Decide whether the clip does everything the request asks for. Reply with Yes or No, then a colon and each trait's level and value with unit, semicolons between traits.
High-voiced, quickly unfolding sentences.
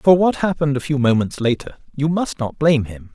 No: medium, 140 Hz; fast, 230 wpm